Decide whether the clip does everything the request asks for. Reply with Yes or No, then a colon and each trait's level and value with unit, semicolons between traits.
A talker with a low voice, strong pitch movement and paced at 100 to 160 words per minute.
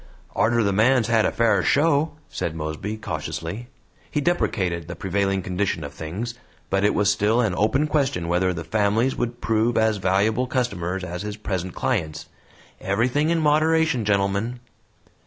No: low, 105 Hz; average, 4.7 semitones; average, 155 wpm